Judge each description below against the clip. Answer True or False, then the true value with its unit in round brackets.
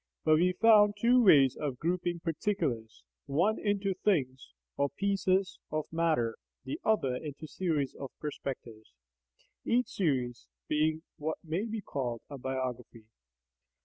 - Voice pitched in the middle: True (155 Hz)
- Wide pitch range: True (6.6 semitones)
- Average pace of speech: False (130 wpm)